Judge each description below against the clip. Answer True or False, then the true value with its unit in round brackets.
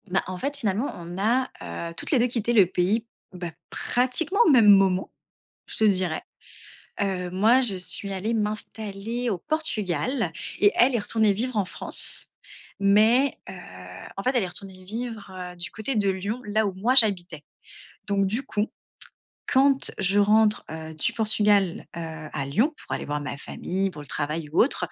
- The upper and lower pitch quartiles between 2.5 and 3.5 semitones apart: False (4.1 semitones)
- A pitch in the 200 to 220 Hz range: True (205 Hz)